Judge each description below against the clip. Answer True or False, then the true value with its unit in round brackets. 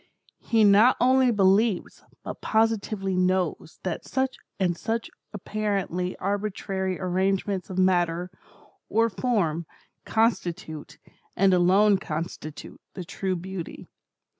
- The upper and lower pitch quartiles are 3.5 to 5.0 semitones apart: False (2.9 semitones)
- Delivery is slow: True (105 wpm)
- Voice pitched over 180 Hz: True (190 Hz)